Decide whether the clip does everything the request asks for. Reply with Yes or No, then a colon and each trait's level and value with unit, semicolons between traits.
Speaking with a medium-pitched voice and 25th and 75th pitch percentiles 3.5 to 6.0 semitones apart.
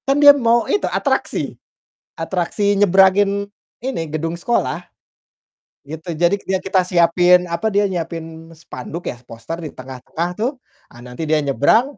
Yes: medium, 175 Hz; average, 3.9 semitones